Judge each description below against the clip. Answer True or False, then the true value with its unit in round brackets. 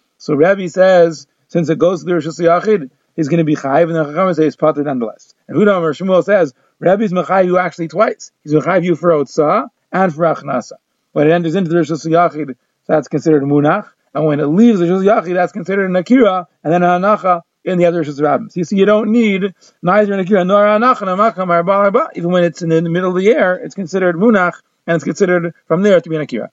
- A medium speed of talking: False (225 wpm)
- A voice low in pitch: False (175 Hz)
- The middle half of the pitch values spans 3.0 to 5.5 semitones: True (3.3 semitones)